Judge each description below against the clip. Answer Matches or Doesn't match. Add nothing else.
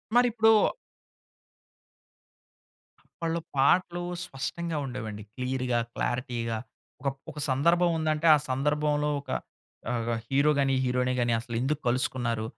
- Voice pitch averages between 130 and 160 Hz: Matches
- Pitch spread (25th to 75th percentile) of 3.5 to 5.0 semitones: Matches